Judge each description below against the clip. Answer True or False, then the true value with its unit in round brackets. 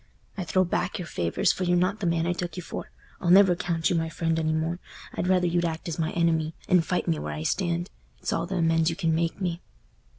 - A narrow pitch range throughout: True (1.7 semitones)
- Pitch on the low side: False (170 Hz)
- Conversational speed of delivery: False (245 wpm)